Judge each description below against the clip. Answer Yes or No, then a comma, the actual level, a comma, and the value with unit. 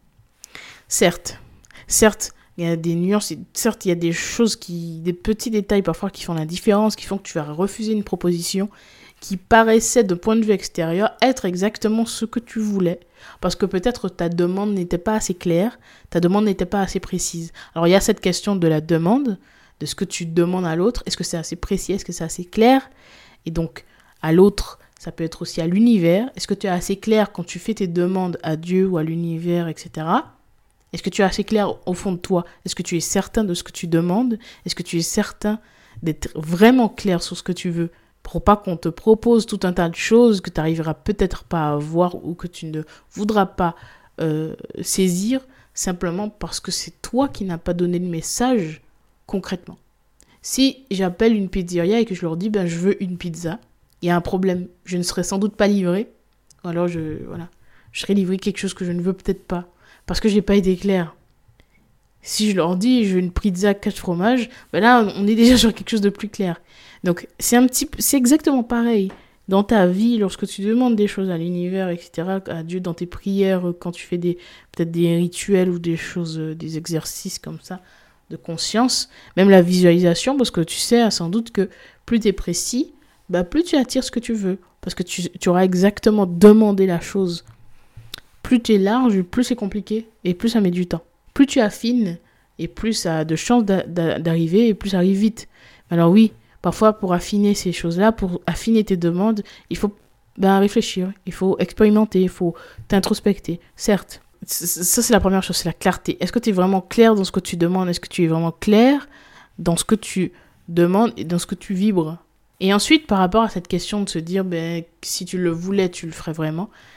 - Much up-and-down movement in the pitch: No, average, 3.6 semitones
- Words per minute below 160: No, fast, 220 wpm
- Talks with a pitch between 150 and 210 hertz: Yes, medium, 185 Hz